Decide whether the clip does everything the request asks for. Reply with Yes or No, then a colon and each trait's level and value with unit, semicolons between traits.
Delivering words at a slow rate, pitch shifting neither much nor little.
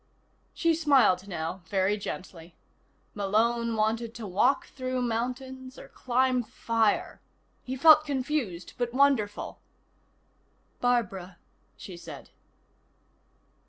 Yes: slow, 95 wpm; average, 4.4 semitones